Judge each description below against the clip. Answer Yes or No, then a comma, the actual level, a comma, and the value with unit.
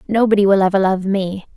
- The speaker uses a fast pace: No, average, 190 wpm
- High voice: Yes, high, 195 Hz